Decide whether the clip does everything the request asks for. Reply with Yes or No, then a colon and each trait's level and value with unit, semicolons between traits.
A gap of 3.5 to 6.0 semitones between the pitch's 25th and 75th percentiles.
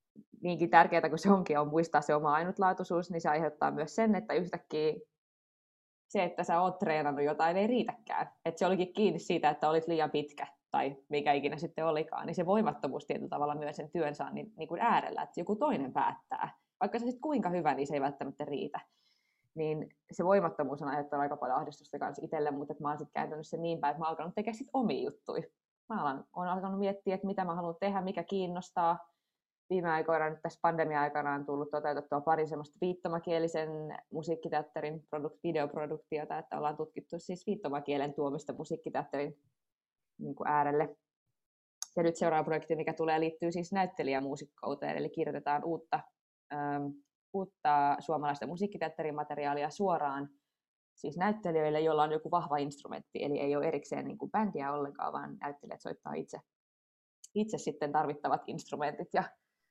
No: average, 3.0 semitones